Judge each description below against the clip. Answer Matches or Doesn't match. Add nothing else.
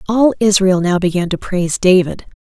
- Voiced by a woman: Matches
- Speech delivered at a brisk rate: Doesn't match